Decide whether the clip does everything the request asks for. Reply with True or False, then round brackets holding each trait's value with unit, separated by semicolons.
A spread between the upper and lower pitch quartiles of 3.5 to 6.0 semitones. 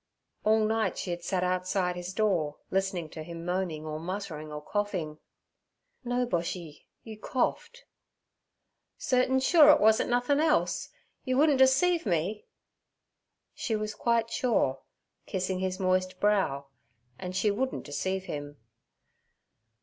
True (5.1 semitones)